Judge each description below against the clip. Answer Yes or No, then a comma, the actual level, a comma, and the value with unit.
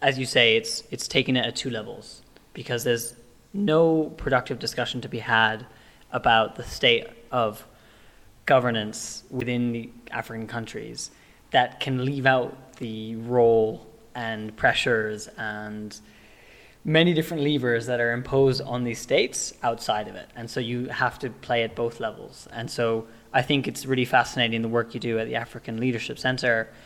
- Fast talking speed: No, average, 165 wpm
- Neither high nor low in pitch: No, low, 120 Hz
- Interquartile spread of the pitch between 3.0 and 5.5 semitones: No, narrow, 2.4 semitones